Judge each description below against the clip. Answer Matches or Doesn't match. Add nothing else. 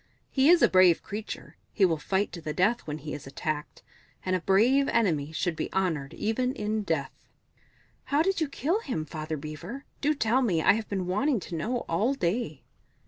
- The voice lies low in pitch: Doesn't match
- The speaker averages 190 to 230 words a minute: Matches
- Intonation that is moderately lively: Doesn't match